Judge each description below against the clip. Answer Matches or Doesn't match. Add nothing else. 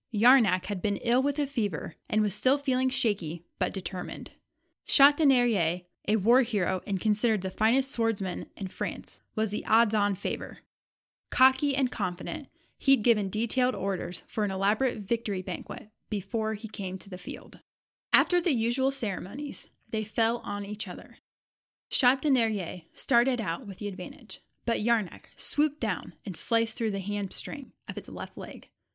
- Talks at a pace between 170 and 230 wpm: Doesn't match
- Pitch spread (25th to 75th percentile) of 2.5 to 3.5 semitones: Doesn't match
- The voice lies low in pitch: Doesn't match